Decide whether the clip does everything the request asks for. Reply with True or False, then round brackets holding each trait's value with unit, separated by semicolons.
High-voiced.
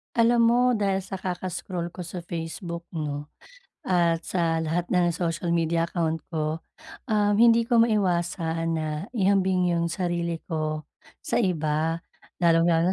False (170 Hz)